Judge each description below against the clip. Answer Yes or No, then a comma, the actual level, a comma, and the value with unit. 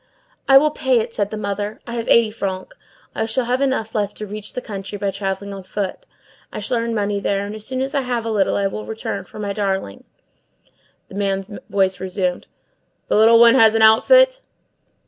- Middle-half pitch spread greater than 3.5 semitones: No, average, 2.8 semitones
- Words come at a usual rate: No, fast, 210 wpm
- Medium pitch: No, high, 215 Hz